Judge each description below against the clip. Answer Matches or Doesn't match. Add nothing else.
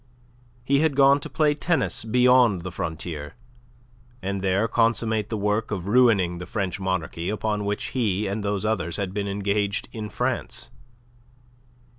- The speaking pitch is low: Matches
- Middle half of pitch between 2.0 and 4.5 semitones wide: Matches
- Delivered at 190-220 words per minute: Doesn't match